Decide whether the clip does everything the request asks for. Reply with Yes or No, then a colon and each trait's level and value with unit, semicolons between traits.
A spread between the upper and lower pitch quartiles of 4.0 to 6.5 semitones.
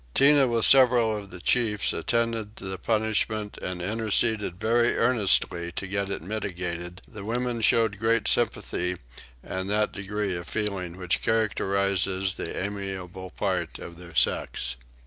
No: average, 3.3 semitones